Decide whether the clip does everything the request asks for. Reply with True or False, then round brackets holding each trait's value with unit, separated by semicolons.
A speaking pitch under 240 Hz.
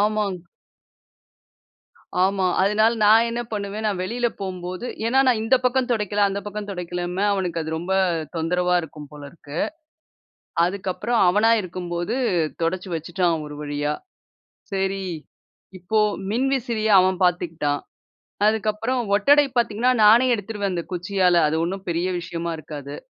True (190 Hz)